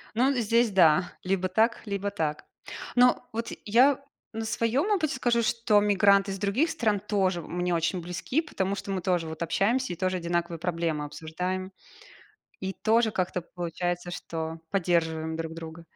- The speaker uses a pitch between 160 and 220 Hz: Yes, high, 190 Hz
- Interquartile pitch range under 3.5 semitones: No, average, 4.5 semitones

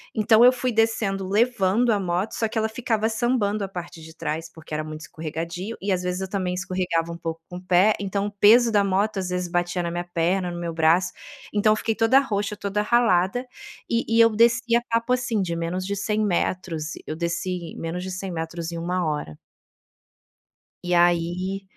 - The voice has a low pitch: No, medium, 185 Hz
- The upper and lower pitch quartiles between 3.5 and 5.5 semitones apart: Yes, average, 3.9 semitones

